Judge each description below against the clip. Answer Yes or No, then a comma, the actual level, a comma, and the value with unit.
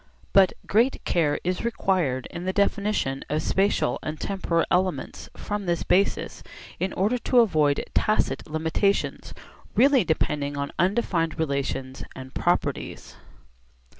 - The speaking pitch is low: No, medium, 180 Hz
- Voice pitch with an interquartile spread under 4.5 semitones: No, average, 4.8 semitones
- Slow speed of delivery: Yes, slow, 125 wpm